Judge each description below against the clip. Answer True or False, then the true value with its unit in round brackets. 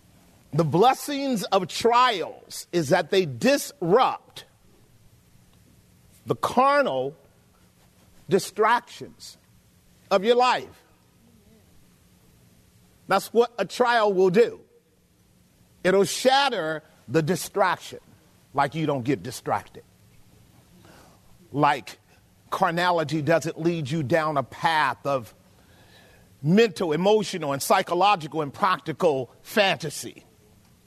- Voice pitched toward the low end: False (175 Hz)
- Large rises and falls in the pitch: True (8.5 semitones)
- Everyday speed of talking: False (85 wpm)